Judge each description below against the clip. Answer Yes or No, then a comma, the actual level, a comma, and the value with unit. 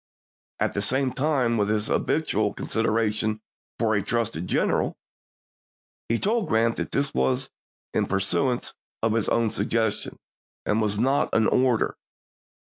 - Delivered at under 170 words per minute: Yes, average, 145 wpm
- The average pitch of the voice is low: Yes, low, 115 Hz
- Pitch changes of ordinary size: Yes, average, 3.0 semitones